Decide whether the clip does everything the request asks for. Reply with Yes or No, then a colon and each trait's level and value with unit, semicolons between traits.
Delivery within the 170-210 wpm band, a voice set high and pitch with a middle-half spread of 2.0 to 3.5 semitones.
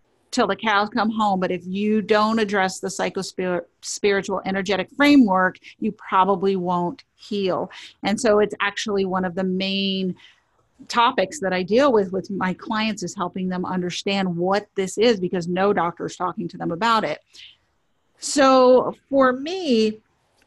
No: average, 160 wpm; high, 195 Hz; average, 2.8 semitones